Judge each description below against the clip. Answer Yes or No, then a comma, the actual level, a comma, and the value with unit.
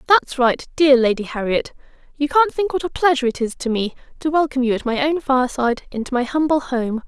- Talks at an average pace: No, fast, 220 wpm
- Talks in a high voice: Yes, very high, 270 Hz